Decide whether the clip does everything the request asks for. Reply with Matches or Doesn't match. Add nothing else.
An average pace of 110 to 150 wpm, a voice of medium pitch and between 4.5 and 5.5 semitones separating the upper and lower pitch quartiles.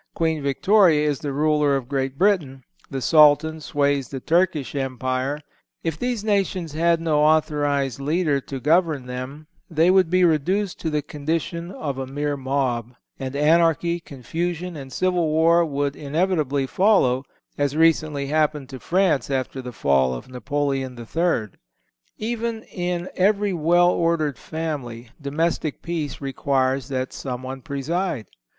Doesn't match